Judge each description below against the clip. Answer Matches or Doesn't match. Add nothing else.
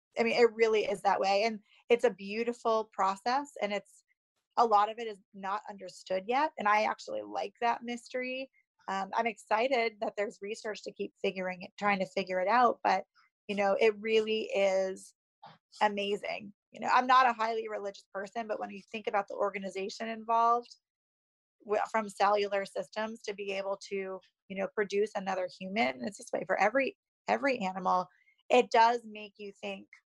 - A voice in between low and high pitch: Doesn't match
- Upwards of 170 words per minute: Matches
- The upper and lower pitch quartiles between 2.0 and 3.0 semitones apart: Matches